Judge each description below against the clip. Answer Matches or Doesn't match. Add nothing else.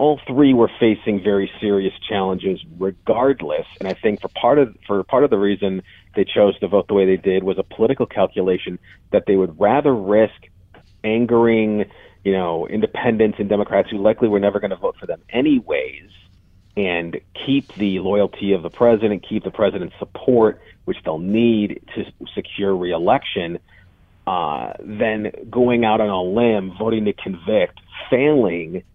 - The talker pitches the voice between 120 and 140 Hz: Doesn't match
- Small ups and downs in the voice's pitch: Doesn't match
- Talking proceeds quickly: Doesn't match